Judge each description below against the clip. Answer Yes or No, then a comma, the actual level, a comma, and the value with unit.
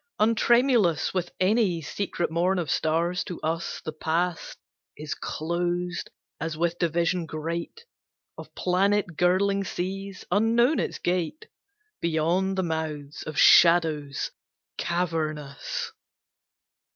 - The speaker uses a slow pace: Yes, slow, 105 wpm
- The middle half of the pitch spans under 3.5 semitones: Yes, average, 3.0 semitones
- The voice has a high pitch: No, medium, 175 Hz